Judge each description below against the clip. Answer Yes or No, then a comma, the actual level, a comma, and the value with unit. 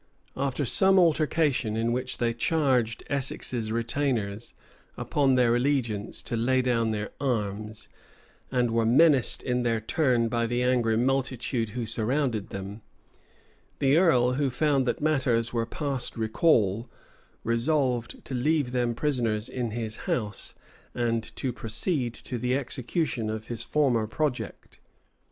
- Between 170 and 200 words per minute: No, slow, 135 wpm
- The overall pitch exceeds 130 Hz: No, low, 120 Hz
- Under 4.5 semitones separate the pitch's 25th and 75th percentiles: Yes, average, 3.1 semitones